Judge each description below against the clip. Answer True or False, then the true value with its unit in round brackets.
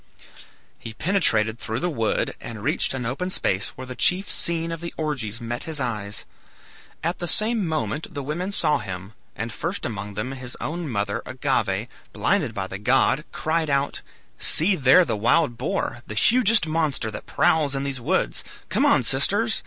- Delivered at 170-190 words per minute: True (175 wpm)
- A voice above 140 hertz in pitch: False (135 Hz)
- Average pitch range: False (6.7 semitones)